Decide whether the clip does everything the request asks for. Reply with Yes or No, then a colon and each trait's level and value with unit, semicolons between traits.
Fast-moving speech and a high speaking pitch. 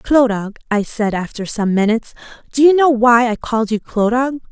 No: average, 175 wpm; high, 235 Hz